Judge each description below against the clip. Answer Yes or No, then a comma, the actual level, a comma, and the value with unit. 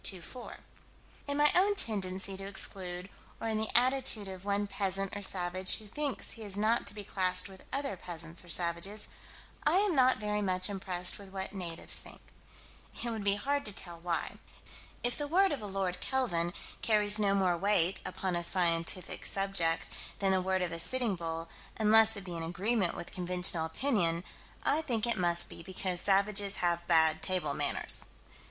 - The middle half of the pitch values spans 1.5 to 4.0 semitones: Yes, average, 3.4 semitones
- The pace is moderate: Yes, average, 180 wpm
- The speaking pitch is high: Yes, high, 195 Hz